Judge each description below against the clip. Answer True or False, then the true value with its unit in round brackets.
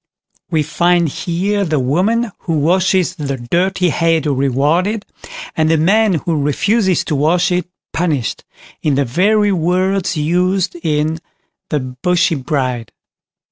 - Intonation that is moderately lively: True (3.8 semitones)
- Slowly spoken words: True (130 wpm)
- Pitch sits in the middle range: True (170 Hz)